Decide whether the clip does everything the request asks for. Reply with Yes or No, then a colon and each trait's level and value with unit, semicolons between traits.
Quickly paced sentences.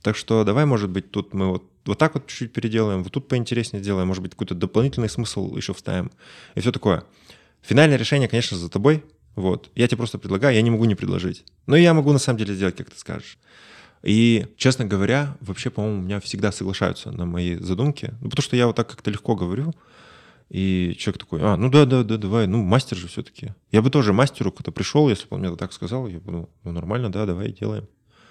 Yes: fast, 225 wpm